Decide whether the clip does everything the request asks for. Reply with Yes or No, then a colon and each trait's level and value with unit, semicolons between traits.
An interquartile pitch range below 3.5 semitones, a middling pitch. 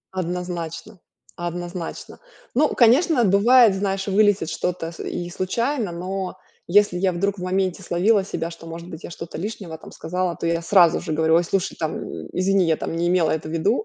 Yes: average, 2.9 semitones; medium, 180 Hz